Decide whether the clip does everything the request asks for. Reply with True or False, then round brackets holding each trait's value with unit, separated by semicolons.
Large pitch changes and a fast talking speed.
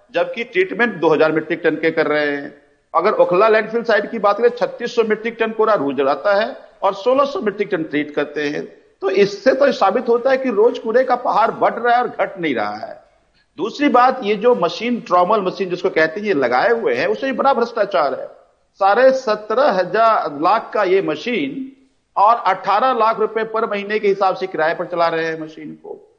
True (5.8 semitones; 215 wpm)